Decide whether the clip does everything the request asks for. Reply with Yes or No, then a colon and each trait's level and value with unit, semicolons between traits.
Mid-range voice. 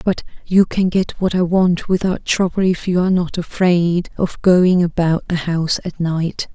Yes: medium, 175 Hz